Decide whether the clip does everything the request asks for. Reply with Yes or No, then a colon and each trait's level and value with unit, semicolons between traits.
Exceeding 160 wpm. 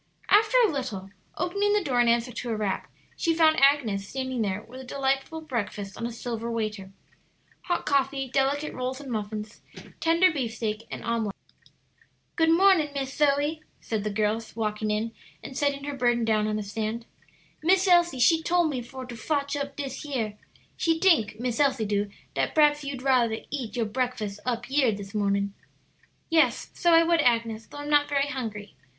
Yes: average, 180 wpm